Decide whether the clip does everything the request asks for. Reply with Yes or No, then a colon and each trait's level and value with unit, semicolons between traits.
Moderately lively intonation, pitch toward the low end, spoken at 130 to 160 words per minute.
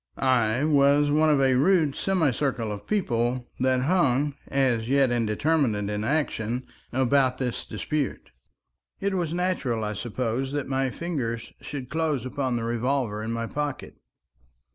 Yes: average, 3.8 semitones; low, 130 Hz; average, 140 wpm